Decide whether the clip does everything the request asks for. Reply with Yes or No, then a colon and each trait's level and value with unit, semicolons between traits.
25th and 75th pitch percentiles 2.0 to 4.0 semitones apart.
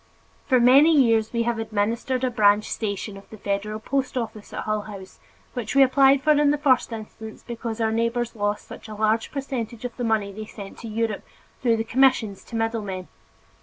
Yes: average, 2.8 semitones